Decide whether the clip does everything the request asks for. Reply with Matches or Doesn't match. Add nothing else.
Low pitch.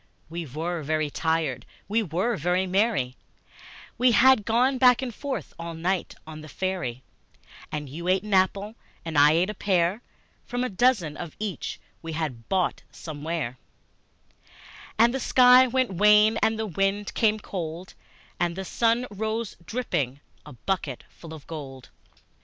Doesn't match